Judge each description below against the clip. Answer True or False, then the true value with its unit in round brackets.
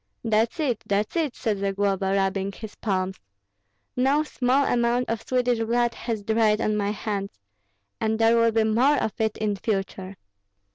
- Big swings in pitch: False (3.0 semitones)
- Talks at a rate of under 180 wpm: True (160 wpm)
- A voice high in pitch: True (220 Hz)